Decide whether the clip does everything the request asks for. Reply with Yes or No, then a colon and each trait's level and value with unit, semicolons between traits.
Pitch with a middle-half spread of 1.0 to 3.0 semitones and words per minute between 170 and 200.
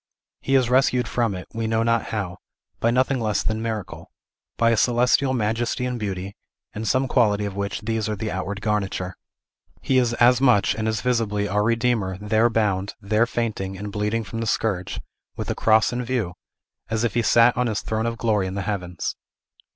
Yes: narrow, 2.6 semitones; average, 195 wpm